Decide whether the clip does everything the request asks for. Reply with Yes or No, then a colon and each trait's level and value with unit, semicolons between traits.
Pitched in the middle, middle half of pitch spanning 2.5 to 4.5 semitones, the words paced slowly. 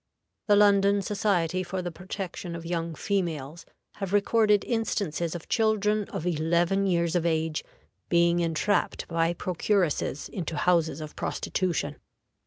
Yes: medium, 175 Hz; average, 3.2 semitones; slow, 130 wpm